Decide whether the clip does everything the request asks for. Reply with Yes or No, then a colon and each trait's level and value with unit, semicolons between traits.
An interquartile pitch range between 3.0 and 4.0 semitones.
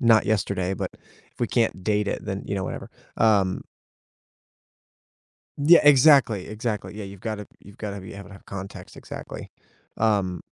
No: narrow, 2.4 semitones